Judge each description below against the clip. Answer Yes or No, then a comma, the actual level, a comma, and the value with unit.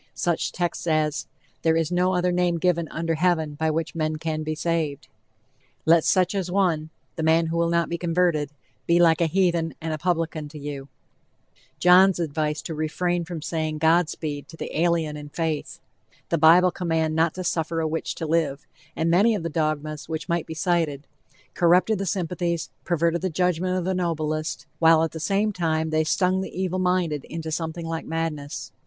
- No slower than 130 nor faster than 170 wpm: No, average, 190 wpm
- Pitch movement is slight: Yes, narrow, 2.1 semitones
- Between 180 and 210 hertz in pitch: No, medium, 165 Hz